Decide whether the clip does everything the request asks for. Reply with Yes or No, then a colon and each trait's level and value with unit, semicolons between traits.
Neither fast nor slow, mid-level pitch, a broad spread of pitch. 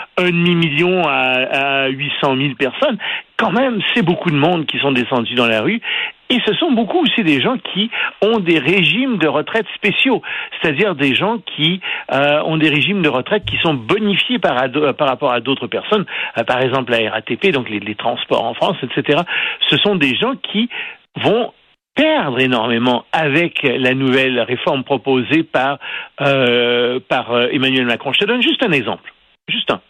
Yes: average, 185 wpm; medium, 145 Hz; wide, 7.2 semitones